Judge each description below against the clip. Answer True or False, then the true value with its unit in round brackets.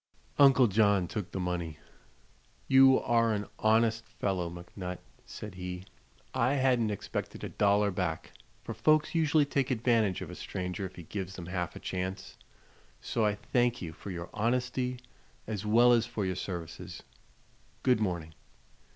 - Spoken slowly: False (155 wpm)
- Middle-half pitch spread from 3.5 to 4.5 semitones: False (4.9 semitones)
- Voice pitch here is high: False (105 Hz)